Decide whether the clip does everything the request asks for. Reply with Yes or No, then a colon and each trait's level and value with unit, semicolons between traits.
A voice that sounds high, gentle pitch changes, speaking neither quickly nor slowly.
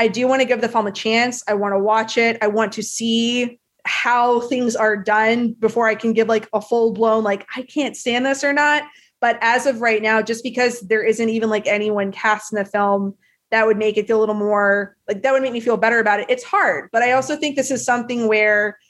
No: high, 225 Hz; narrow, 2.3 semitones; fast, 255 wpm